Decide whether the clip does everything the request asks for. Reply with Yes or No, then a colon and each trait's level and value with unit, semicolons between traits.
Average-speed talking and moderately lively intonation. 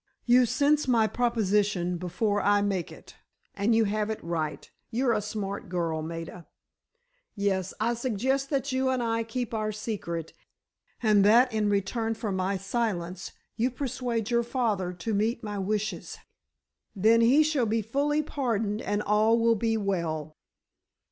Yes: average, 150 wpm; average, 3.2 semitones